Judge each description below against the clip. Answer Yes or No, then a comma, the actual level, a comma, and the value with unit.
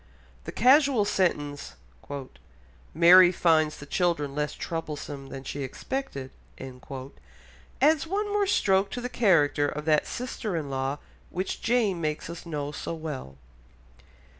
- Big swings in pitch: Yes, wide, 6.0 semitones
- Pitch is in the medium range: Yes, medium, 160 Hz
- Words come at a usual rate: No, slow, 130 wpm